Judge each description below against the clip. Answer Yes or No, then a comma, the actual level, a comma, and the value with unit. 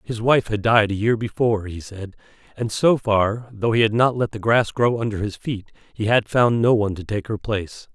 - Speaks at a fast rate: Yes, fast, 240 wpm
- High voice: No, low, 110 Hz